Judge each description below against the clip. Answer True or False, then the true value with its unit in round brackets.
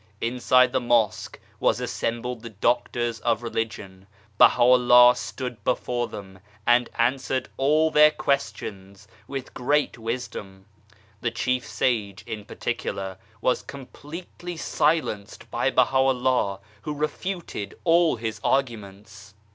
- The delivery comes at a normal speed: False (115 wpm)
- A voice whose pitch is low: True (120 Hz)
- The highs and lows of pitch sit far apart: False (3.8 semitones)